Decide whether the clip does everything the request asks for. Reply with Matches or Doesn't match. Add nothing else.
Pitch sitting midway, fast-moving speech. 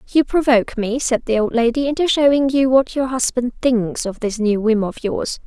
Doesn't match